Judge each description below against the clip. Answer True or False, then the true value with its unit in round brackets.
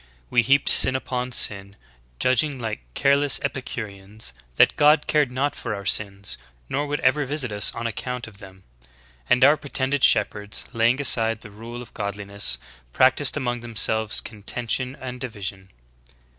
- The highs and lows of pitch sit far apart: False (4.3 semitones)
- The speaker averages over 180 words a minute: False (155 wpm)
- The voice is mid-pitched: False (120 Hz)